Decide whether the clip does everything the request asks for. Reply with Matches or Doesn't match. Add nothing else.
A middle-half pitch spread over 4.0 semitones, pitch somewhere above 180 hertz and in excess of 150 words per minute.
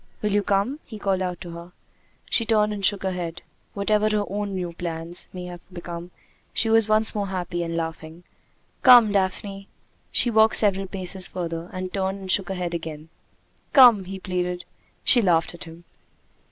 Doesn't match